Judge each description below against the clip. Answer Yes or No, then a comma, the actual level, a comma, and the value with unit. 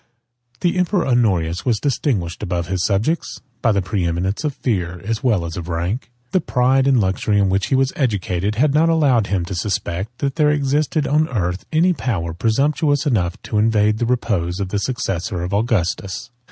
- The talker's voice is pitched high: No, low, 110 Hz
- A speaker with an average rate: Yes, average, 190 wpm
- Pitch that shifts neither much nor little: No, wide, 6.6 semitones